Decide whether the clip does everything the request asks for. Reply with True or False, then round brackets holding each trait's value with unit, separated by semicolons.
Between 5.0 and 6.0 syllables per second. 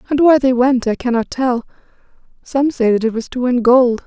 True (5.2 syllables/s)